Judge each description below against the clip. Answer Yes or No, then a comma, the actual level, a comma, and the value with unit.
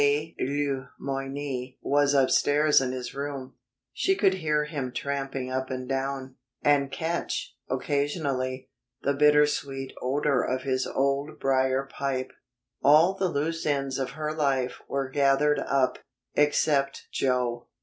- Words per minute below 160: Yes, average, 140 wpm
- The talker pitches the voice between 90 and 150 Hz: Yes, medium, 140 Hz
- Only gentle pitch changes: Yes, narrow, 1.8 semitones